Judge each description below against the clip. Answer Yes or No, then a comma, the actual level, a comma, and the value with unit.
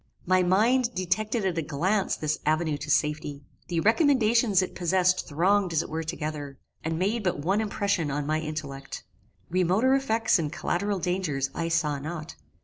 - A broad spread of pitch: No, average, 4.7 semitones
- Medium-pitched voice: Yes, medium, 175 Hz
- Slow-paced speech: No, average, 165 wpm